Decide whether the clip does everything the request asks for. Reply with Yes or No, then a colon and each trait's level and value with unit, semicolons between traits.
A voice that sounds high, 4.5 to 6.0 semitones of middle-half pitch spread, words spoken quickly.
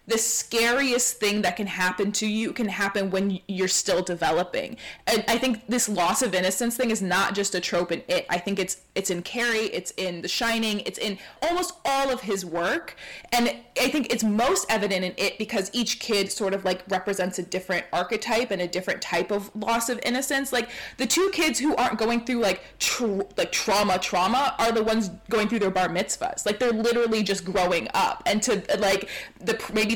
No: high, 210 Hz; average, 3.9 semitones; fast, 210 wpm